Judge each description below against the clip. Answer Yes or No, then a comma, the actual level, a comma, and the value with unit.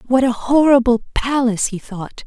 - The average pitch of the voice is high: Yes, high, 245 Hz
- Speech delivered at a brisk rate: No, average, 160 wpm